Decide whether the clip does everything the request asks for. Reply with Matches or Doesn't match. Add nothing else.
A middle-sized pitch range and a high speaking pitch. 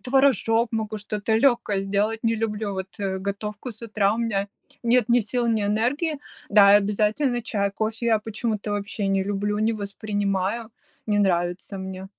Doesn't match